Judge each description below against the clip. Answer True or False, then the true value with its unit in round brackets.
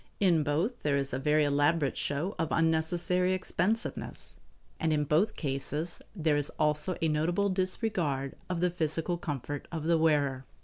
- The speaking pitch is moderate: True (160 Hz)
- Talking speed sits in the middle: True (160 wpm)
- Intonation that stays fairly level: False (3.4 semitones)